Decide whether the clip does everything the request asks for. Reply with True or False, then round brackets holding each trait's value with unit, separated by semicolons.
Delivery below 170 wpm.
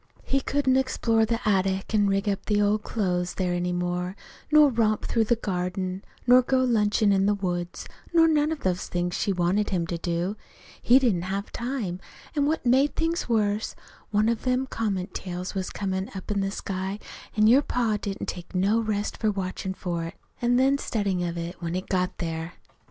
False (200 wpm)